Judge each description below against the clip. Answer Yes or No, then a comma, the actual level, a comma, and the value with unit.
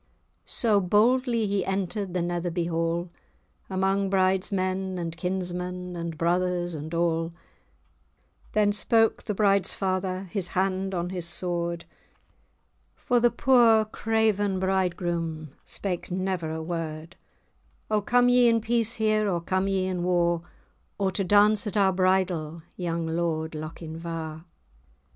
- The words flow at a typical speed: No, slow, 130 wpm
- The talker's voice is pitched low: No, medium, 185 Hz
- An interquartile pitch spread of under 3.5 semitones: Yes, average, 2.8 semitones